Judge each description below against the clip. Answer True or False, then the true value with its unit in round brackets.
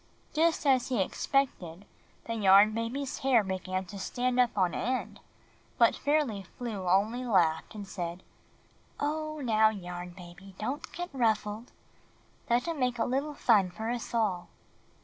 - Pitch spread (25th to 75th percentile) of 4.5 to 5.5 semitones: True (5.0 semitones)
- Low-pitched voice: False (220 Hz)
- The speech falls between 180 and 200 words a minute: False (150 wpm)